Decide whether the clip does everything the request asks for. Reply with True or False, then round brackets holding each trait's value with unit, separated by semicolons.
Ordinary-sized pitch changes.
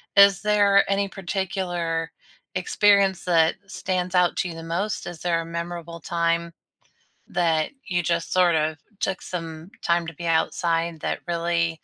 False (2.1 semitones)